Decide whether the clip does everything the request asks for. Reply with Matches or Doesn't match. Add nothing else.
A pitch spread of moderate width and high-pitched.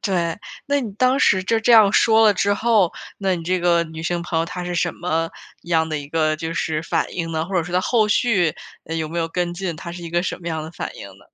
Doesn't match